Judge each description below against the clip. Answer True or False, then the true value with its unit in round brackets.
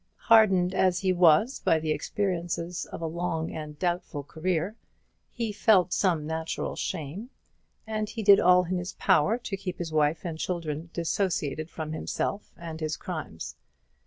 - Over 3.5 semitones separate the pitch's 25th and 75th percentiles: False (3.2 semitones)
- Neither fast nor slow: True (160 wpm)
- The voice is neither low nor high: True (175 Hz)